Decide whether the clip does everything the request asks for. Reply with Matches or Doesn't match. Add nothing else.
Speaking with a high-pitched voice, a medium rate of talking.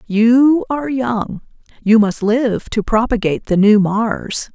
Matches